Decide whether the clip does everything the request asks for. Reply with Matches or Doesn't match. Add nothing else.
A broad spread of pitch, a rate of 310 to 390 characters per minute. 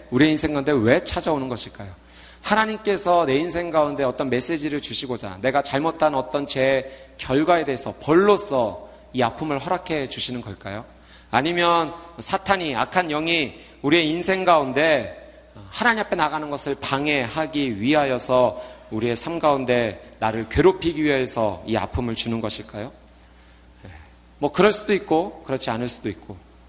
Matches